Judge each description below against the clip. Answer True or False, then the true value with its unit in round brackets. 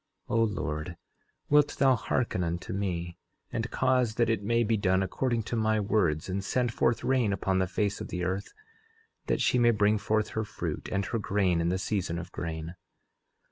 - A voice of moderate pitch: False (100 Hz)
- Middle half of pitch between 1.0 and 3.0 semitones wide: False (4.0 semitones)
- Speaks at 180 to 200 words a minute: True (195 wpm)